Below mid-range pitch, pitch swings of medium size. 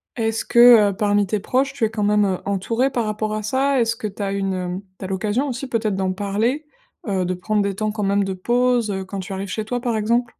No: high, 215 Hz; average, 3.3 semitones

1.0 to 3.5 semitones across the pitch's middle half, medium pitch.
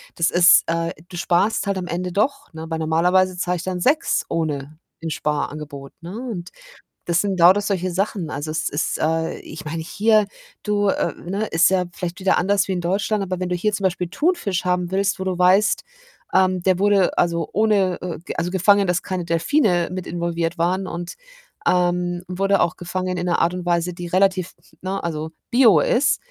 Yes: narrow, 2.4 semitones; medium, 180 Hz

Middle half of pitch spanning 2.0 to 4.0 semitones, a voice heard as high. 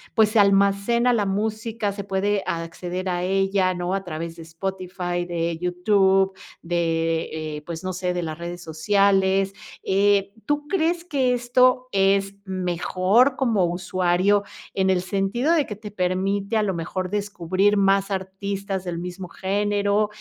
Yes: narrow, 2.4 semitones; high, 195 Hz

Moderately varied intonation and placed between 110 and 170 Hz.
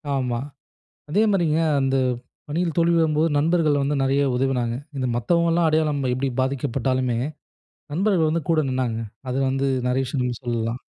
Yes: average, 4.1 semitones; medium, 140 Hz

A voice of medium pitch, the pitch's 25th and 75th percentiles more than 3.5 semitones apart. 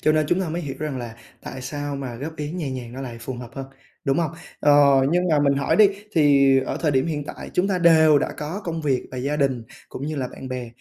No: medium, 145 Hz; average, 2.9 semitones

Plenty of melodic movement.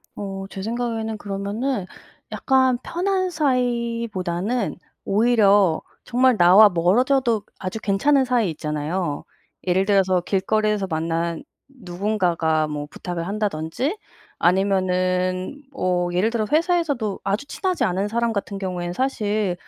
No: average, 4.8 semitones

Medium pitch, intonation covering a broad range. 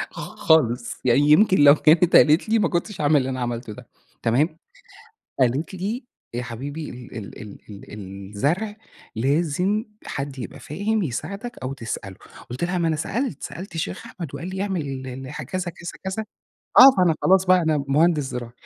Yes: medium, 150 Hz; wide, 6.5 semitones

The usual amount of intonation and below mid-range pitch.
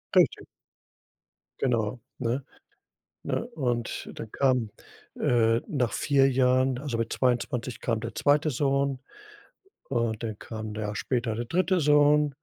Yes: average, 3.2 semitones; low, 125 Hz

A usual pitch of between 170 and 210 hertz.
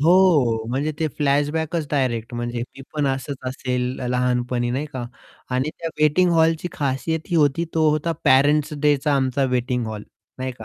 No: medium, 140 Hz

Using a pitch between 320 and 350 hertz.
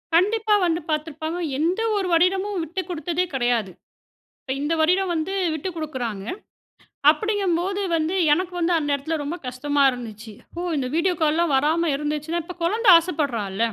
Yes: very high, 325 Hz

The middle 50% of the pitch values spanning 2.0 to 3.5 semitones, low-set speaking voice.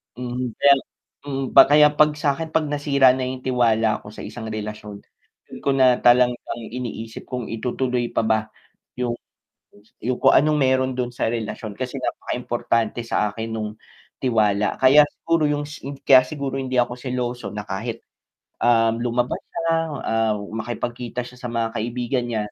Yes: narrow, 2.6 semitones; low, 125 Hz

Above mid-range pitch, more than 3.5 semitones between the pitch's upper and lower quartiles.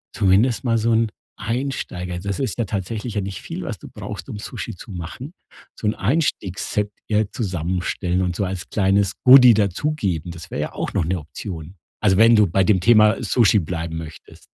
No: low, 100 Hz; average, 4.0 semitones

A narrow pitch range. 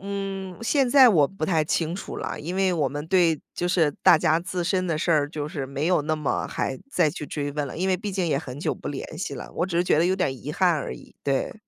No: average, 3.9 semitones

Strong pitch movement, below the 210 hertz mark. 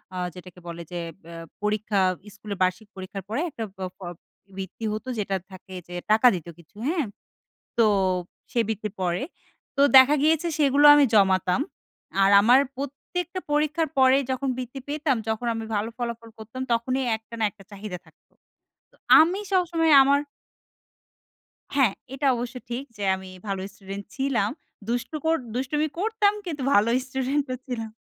No: wide, 5.9 semitones; high, 235 Hz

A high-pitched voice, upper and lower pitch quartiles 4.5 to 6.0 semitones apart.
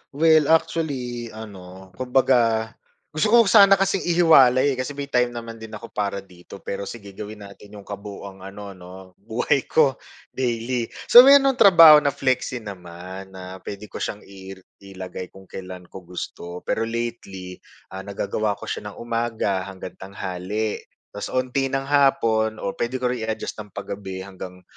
No: low, 110 Hz; average, 5.2 semitones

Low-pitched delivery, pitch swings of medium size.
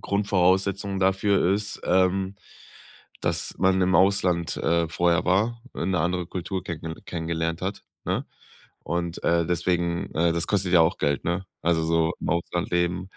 No: very low, 90 Hz; narrow, 2.1 semitones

